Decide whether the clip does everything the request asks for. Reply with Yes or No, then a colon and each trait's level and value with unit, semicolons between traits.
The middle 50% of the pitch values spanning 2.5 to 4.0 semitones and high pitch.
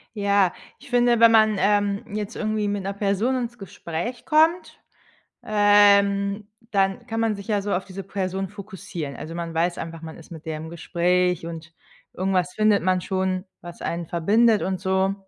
Yes: average, 2.9 semitones; high, 195 Hz